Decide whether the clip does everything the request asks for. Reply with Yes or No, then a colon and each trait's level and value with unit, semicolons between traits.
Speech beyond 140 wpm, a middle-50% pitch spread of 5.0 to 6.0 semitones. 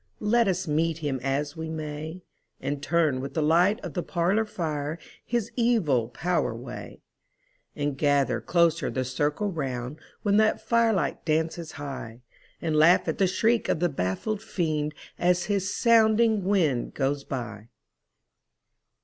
Yes: average, 150 wpm; average, 5.3 semitones